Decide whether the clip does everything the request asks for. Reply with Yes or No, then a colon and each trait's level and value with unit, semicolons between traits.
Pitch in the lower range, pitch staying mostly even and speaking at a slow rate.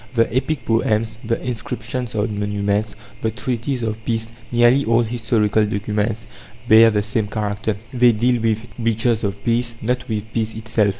No: low, 110 Hz; narrow, 1.8 semitones; average, 160 wpm